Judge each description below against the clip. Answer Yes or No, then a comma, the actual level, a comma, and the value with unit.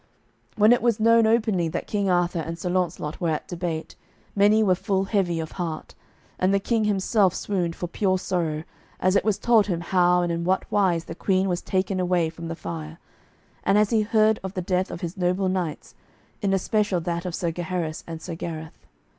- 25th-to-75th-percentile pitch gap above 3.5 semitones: No, average, 3.0 semitones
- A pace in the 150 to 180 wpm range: No, fast, 205 wpm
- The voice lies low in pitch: No, medium, 185 Hz